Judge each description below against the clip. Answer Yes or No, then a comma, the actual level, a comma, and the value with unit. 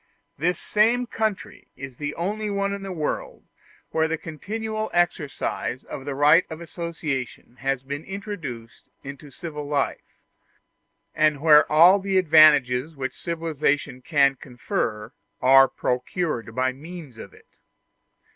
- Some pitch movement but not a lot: Yes, average, 4.8 semitones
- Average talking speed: No, slow, 130 wpm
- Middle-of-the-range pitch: Yes, medium, 155 Hz